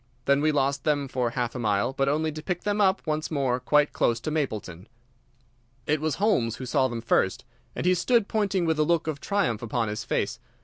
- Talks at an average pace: No, fast, 220 wpm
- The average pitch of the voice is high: No, medium, 145 Hz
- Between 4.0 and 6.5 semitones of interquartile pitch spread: Yes, average, 4.9 semitones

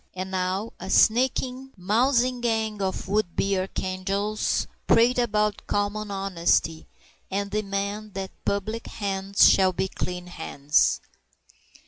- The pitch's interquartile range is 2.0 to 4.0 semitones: Yes, narrow, 2.4 semitones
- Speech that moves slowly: Yes, slow, 115 wpm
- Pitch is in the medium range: No, high, 200 Hz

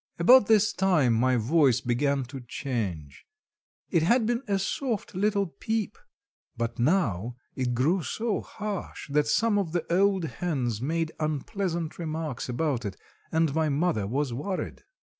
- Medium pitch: Yes, medium, 155 Hz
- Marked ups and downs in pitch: Yes, wide, 7.2 semitones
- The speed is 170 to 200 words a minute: No, average, 145 wpm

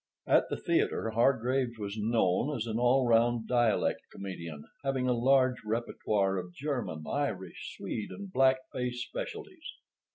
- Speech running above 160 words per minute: No, average, 140 wpm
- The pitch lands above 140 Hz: No, low, 120 Hz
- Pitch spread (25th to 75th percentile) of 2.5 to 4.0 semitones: Yes, average, 3.6 semitones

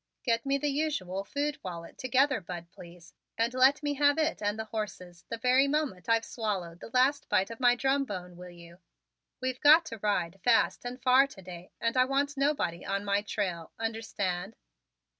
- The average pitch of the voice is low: No, high, 225 Hz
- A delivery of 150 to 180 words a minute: No, average, 190 wpm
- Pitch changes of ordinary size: No, wide, 6.8 semitones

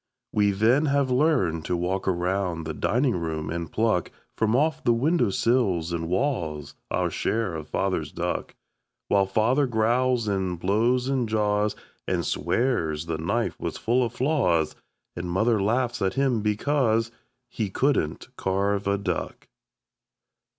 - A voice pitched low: Yes, low, 105 Hz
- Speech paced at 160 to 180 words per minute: No, average, 145 wpm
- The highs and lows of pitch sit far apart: Yes, wide, 5.8 semitones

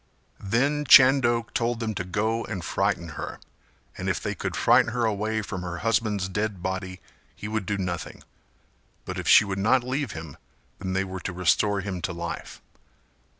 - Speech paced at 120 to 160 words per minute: No, average, 180 wpm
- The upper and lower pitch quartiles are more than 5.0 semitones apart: No, average, 3.6 semitones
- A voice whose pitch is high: No, low, 100 Hz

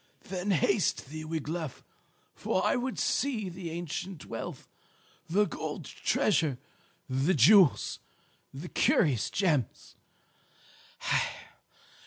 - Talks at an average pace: No, slow, 95 wpm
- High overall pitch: No, medium, 170 Hz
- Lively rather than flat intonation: No, average, 4.7 semitones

